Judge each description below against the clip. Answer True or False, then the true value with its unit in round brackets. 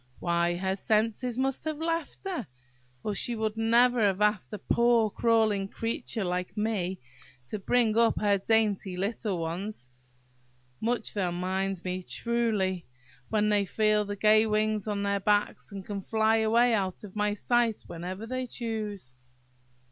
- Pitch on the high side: True (210 Hz)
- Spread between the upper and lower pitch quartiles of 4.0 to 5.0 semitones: False (2.8 semitones)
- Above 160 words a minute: False (155 wpm)